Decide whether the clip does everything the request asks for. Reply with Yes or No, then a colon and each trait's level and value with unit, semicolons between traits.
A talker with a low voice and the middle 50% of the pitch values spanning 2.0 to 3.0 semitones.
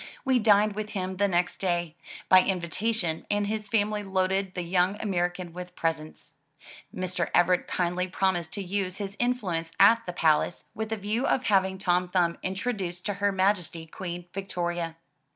No: medium, 185 Hz; narrow, 2.6 semitones